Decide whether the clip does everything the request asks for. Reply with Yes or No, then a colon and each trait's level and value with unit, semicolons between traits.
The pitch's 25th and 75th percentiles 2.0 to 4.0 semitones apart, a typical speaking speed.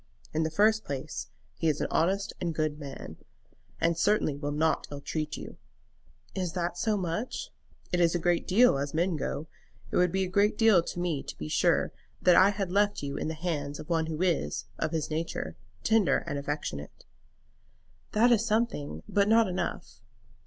No: average, 4.6 semitones; average, 190 wpm